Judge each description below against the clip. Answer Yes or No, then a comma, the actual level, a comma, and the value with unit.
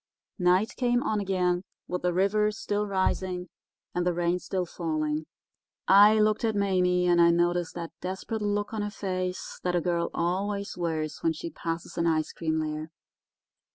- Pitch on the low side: No, medium, 180 Hz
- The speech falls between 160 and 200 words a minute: Yes, average, 170 wpm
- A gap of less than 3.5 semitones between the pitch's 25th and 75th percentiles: Yes, average, 2.9 semitones